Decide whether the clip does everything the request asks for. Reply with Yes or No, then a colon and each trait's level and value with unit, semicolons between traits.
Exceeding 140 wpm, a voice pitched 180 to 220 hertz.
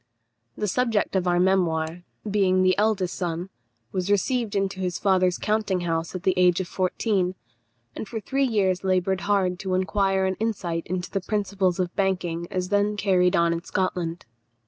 Yes: average, 170 wpm; medium, 185 Hz